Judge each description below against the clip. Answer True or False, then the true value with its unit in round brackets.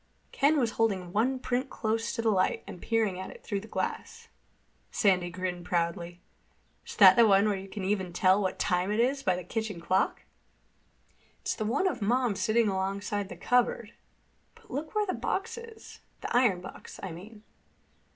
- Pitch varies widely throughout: False (4.6 semitones)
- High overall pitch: True (210 Hz)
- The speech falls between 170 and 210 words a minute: True (180 wpm)